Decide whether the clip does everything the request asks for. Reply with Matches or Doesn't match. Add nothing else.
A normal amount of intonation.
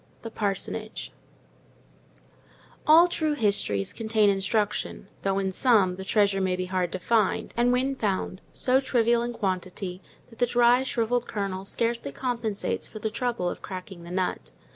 Matches